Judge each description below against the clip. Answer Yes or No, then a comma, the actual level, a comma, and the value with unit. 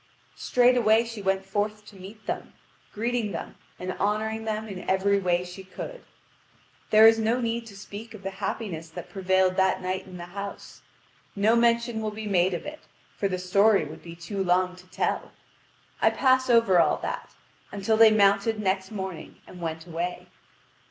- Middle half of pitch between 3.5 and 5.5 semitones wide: No, average, 3.1 semitones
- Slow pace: No, average, 180 wpm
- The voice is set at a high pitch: Yes, high, 200 Hz